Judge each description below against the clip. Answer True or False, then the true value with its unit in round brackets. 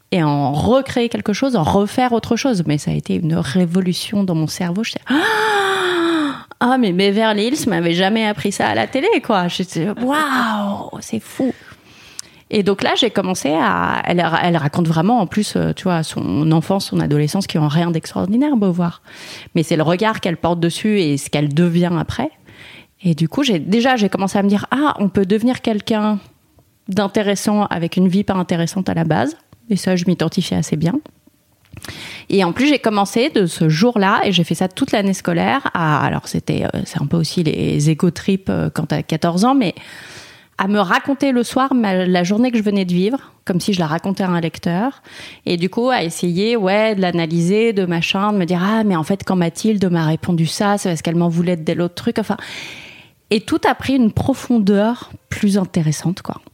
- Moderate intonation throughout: True (4.7 semitones)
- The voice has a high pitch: True (195 Hz)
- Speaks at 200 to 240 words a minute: True (205 wpm)